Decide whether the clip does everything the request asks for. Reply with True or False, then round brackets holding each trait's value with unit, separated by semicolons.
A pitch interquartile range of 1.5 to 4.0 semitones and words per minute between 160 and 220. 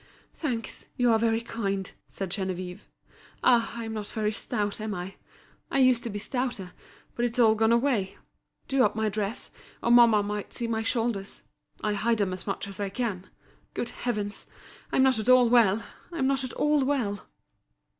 True (3.1 semitones; 180 wpm)